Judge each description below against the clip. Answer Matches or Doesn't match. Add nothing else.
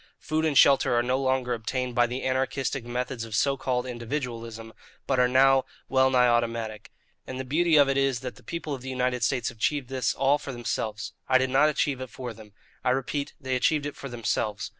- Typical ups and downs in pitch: Doesn't match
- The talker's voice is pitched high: Doesn't match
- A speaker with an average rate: Doesn't match